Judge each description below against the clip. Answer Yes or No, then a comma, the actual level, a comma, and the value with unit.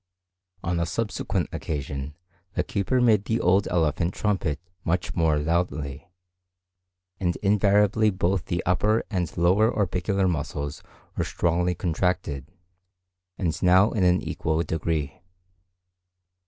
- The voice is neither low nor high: No, very low, 90 Hz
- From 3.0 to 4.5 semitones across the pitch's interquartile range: Yes, average, 3.5 semitones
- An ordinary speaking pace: No, slow, 115 wpm